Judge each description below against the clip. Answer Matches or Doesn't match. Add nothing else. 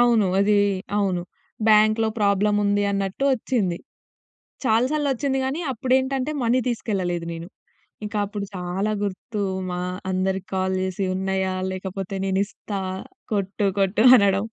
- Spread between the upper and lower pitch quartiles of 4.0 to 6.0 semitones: Doesn't match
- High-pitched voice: Matches